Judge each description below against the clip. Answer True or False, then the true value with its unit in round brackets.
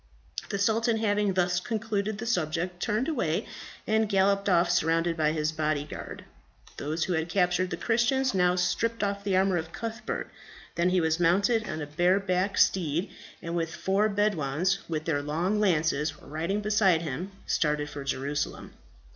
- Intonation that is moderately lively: True (4.3 semitones)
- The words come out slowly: False (165 wpm)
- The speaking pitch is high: False (180 Hz)